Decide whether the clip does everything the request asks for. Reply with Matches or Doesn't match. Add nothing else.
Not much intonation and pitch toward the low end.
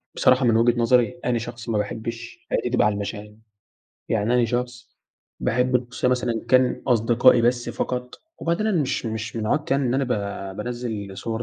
Matches